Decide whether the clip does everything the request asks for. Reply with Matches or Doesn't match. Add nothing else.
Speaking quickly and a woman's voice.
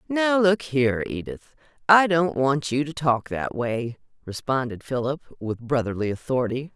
Doesn't match